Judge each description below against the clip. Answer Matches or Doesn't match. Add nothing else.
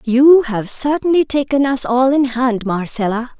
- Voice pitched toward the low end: Doesn't match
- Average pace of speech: Matches